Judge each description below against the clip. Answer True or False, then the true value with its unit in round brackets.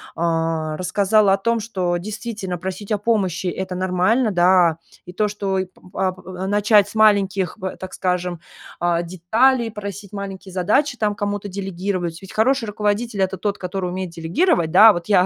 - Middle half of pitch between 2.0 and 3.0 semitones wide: True (2.6 semitones)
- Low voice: False (190 Hz)